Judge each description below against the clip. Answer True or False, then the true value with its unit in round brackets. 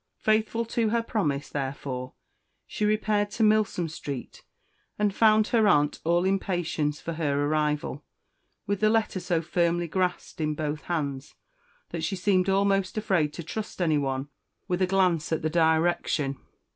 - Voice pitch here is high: False (175 Hz)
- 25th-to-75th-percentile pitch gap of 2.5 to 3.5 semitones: False (5.2 semitones)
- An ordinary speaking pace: True (150 wpm)